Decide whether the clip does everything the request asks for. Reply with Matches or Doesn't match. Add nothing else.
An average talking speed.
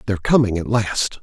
Matches